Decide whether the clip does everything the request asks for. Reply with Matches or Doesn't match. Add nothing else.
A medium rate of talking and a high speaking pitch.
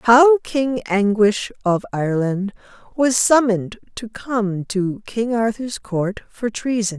Doesn't match